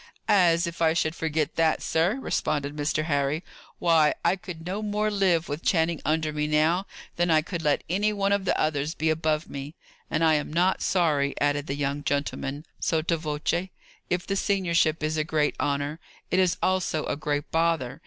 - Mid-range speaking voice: Yes, medium, 160 Hz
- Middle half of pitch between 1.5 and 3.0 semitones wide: Yes, average, 2.7 semitones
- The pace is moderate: Yes, average, 190 wpm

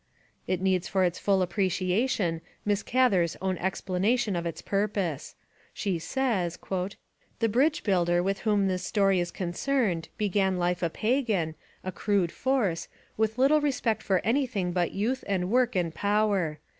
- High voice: Yes, high, 195 Hz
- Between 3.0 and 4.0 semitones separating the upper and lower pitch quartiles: Yes, average, 3.6 semitones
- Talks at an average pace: Yes, average, 155 wpm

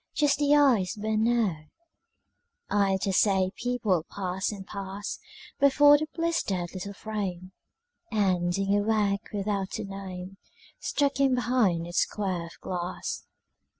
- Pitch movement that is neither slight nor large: Yes, average, 4.1 semitones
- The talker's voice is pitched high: Yes, high, 200 Hz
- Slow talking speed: Yes, slow, 130 wpm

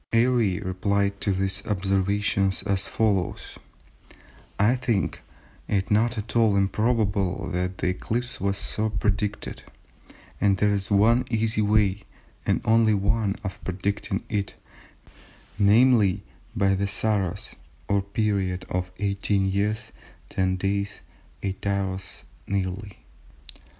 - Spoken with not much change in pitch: Yes, narrow, 1.7 semitones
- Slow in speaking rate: Yes, slow, 110 wpm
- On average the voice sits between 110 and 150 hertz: No, low, 100 Hz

